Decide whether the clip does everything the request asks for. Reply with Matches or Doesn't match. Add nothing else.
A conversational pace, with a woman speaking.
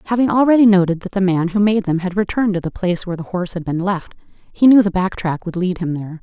Doesn't match